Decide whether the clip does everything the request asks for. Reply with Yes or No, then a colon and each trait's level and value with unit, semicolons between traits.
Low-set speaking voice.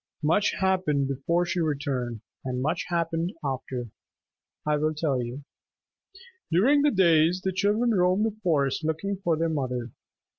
No: medium, 160 Hz